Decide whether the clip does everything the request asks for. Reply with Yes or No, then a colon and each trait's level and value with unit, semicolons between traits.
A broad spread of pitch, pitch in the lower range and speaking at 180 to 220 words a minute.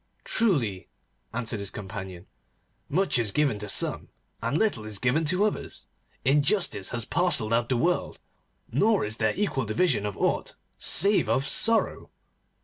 No: wide, 8.9 semitones; low, 125 Hz; average, 145 wpm